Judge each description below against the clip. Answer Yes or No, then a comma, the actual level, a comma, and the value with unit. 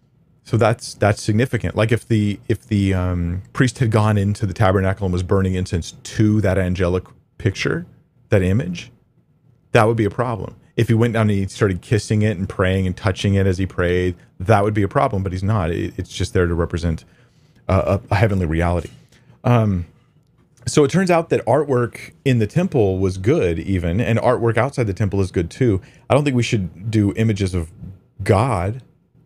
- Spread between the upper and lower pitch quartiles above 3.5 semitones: Yes, average, 4.1 semitones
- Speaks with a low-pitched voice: Yes, low, 105 Hz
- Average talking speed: Yes, average, 195 wpm